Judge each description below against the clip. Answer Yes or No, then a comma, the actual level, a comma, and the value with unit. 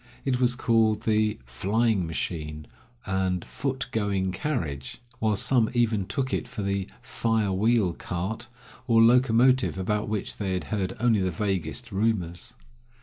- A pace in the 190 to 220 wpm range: No, average, 145 wpm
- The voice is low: Yes, low, 105 Hz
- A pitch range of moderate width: Yes, average, 3.6 semitones